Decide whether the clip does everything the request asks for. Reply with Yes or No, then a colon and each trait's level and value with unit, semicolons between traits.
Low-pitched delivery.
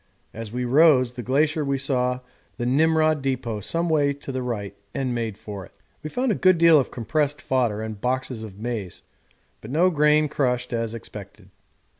Yes: low, 130 Hz